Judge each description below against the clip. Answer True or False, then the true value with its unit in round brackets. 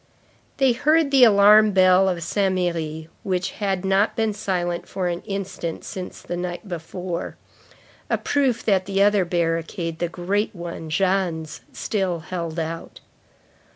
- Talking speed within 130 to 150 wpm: True (145 wpm)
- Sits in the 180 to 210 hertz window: True (185 Hz)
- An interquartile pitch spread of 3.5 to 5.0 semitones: False (2.9 semitones)